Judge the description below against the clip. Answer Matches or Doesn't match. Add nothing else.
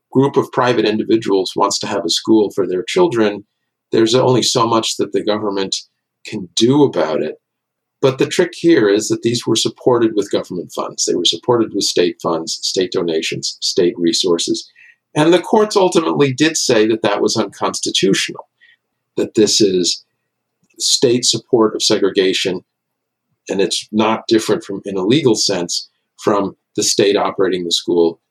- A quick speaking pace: Doesn't match